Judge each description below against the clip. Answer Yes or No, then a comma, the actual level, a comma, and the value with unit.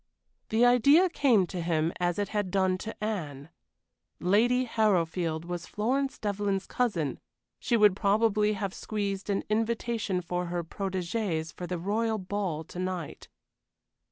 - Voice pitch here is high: Yes, high, 200 Hz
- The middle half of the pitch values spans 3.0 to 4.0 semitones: Yes, average, 3.7 semitones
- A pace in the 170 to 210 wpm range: No, average, 140 wpm